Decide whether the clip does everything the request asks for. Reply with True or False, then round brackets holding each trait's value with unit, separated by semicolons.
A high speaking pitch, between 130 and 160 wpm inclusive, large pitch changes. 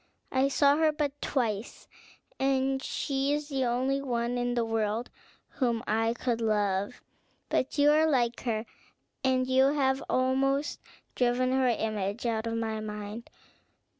False (250 Hz; 145 wpm; 3.2 semitones)